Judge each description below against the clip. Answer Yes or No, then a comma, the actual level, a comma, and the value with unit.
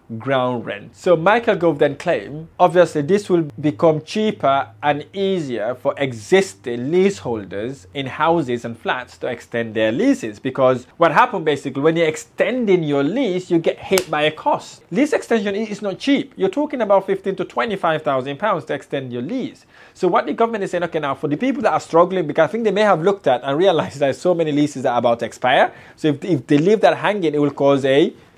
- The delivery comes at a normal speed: No, fast, 210 wpm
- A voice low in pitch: No, medium, 160 Hz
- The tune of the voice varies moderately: No, wide, 5.8 semitones